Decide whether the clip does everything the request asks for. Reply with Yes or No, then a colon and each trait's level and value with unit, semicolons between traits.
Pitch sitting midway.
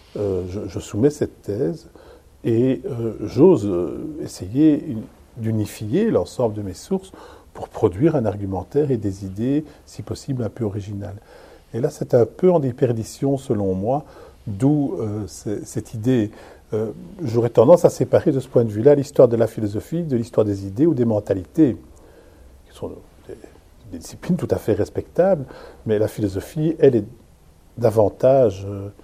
No: low, 115 Hz